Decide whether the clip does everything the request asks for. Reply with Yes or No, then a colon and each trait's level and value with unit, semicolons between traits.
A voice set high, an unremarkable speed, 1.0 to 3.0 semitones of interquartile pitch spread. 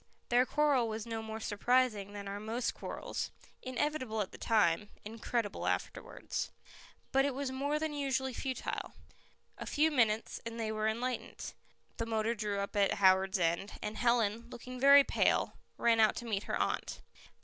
No: high, 230 Hz; average, 165 wpm; average, 3.4 semitones